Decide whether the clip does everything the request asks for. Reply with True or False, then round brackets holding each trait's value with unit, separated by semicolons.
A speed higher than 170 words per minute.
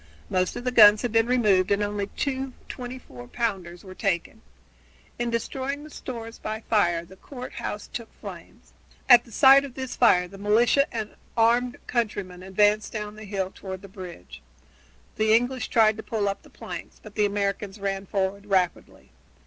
True (180 wpm)